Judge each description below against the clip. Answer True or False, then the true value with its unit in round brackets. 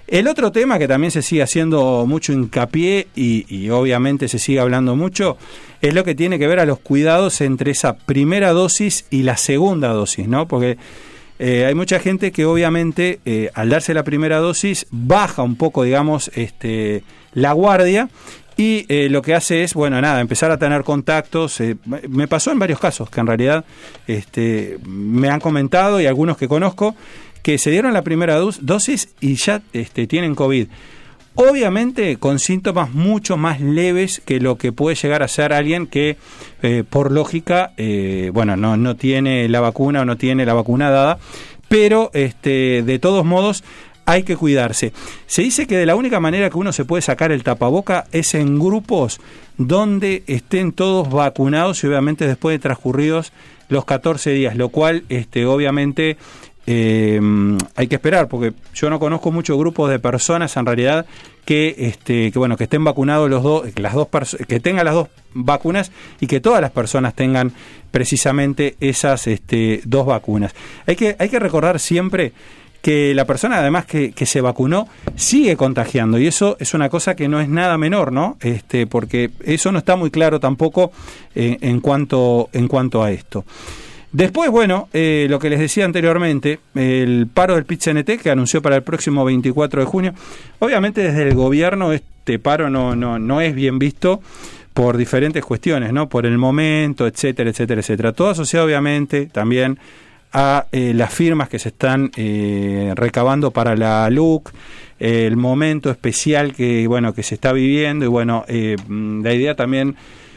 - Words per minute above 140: True (175 wpm)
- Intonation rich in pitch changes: False (5.0 semitones)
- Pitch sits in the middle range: True (145 Hz)